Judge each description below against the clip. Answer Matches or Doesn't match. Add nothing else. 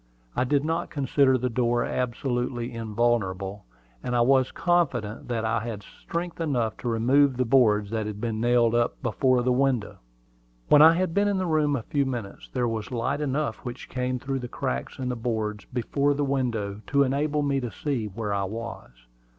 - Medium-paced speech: Matches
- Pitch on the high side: Doesn't match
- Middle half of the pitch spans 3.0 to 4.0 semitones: Matches